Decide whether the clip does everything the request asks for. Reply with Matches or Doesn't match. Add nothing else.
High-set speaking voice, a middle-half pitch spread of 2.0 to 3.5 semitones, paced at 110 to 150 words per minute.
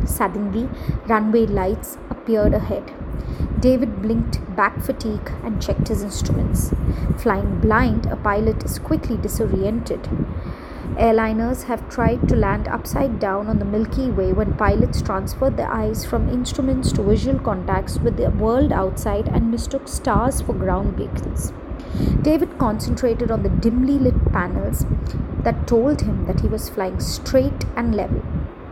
Matches